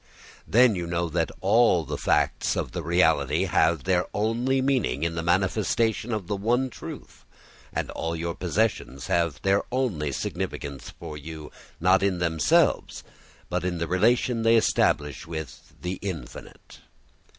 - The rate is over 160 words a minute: No, average, 150 wpm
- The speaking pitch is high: No, very low, 90 Hz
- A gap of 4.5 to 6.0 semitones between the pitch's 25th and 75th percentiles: Yes, average, 5.2 semitones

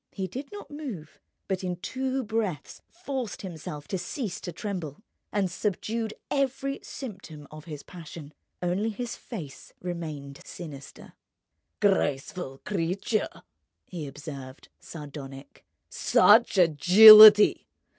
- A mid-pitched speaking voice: Yes, medium, 180 Hz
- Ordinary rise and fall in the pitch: No, wide, 6.3 semitones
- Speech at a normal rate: No, slow, 110 wpm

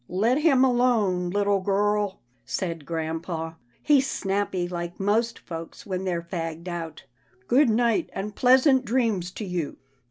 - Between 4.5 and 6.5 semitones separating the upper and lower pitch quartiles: Yes, wide, 5.4 semitones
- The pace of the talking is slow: No, average, 150 wpm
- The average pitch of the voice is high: Yes, high, 195 Hz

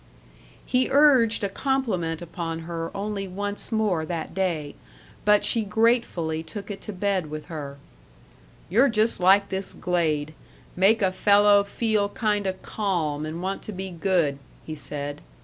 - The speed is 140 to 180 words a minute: Yes, average, 150 wpm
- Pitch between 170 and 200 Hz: Yes, high, 190 Hz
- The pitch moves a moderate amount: Yes, average, 4.2 semitones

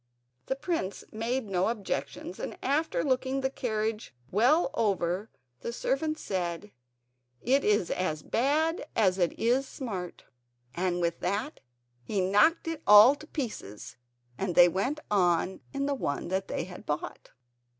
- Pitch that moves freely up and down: Yes, wide, 6.6 semitones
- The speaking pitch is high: Yes, high, 210 Hz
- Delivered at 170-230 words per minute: No, average, 145 wpm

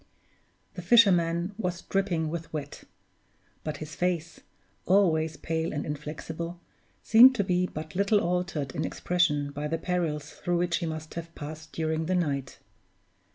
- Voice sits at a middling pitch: Yes, medium, 165 Hz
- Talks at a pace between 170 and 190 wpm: No, average, 150 wpm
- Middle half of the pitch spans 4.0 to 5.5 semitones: No, narrow, 2.5 semitones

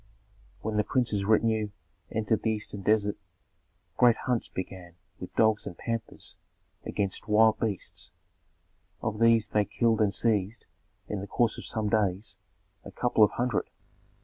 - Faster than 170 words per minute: No, average, 145 wpm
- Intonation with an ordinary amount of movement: No, narrow, 1.8 semitones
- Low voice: Yes, low, 110 Hz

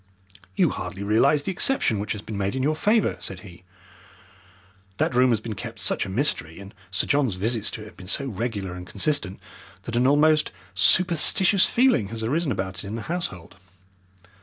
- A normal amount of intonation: No, wide, 6.7 semitones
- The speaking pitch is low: Yes, low, 115 Hz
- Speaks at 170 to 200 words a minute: Yes, average, 190 wpm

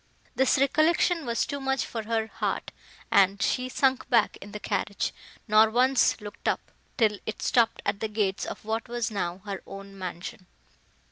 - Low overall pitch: No, high, 220 Hz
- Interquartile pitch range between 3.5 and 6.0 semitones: Yes, average, 3.9 semitones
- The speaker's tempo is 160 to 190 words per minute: Yes, average, 175 wpm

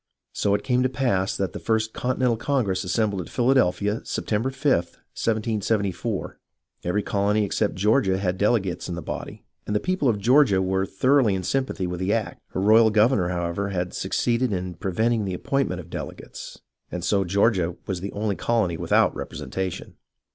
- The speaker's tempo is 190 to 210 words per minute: No, average, 175 wpm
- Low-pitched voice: Yes, low, 105 Hz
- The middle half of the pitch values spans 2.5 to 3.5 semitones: No, average, 3.9 semitones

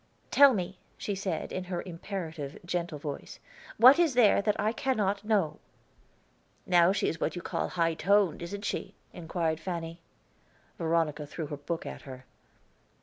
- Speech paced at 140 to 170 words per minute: Yes, average, 155 wpm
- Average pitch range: Yes, average, 3.7 semitones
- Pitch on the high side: No, medium, 175 Hz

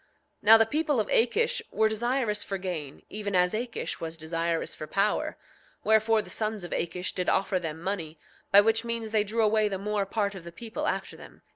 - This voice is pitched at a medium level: No, high, 210 Hz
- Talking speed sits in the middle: No, fast, 210 wpm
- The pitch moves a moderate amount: Yes, average, 3.8 semitones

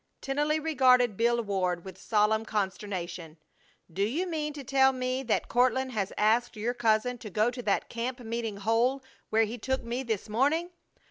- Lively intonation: No, average, 3.6 semitones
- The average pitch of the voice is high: Yes, high, 235 Hz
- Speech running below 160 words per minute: No, average, 175 wpm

